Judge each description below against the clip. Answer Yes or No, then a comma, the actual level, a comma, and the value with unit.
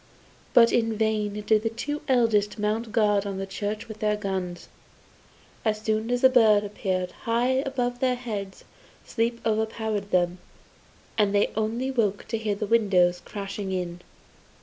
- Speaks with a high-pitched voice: Yes, high, 215 Hz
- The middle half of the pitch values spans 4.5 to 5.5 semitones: No, narrow, 2.4 semitones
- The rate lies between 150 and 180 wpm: Yes, average, 155 wpm